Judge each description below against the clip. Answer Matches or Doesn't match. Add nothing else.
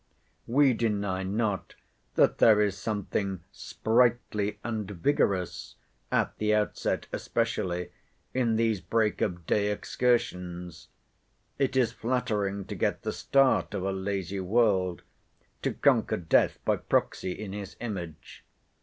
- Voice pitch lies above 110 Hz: Doesn't match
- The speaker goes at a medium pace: Doesn't match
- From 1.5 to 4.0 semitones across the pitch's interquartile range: Matches